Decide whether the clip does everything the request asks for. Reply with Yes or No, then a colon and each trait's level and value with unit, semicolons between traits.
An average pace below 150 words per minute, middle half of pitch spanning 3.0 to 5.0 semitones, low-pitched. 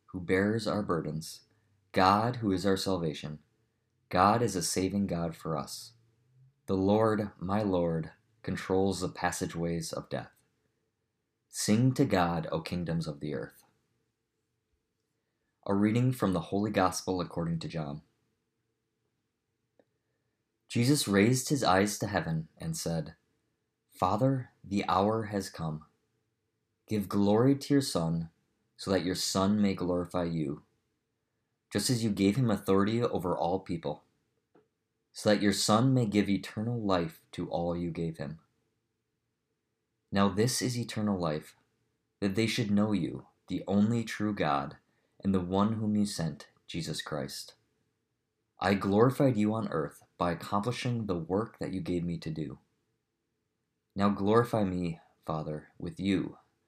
Yes: average, 140 wpm; average, 3.8 semitones; low, 100 Hz